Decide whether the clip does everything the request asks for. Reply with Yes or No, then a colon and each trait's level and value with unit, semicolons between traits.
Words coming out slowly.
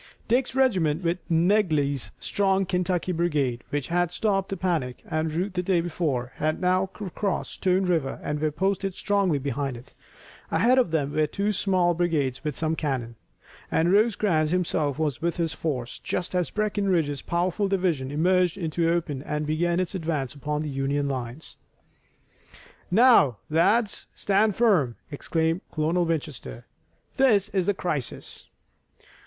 No: average, 150 wpm